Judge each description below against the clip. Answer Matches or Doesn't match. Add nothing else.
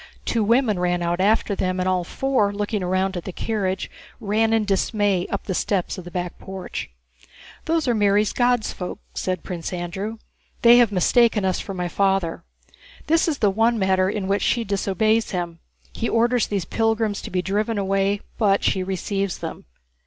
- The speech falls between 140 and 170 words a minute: Doesn't match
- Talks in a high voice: Matches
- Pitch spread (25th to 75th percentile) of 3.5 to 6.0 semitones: Doesn't match